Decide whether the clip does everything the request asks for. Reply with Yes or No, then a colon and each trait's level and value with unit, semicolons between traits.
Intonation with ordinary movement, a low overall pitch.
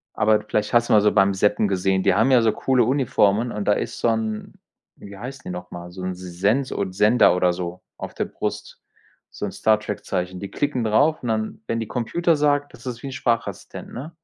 Yes: average, 4.1 semitones; low, 110 Hz